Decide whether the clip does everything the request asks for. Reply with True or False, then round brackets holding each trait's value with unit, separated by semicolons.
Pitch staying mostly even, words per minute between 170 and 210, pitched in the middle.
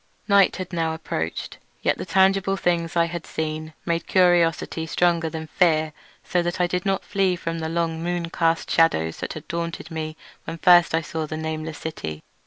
True (1.7 semitones; 190 wpm; 165 Hz)